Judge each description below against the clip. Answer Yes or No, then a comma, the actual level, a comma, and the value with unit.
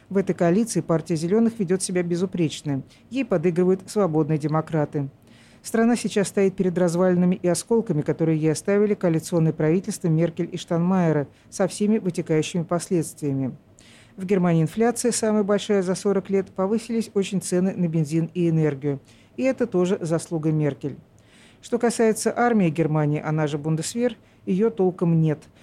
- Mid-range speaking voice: Yes, medium, 175 Hz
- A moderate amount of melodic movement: Yes, average, 4.1 semitones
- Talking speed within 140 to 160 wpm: Yes, average, 145 wpm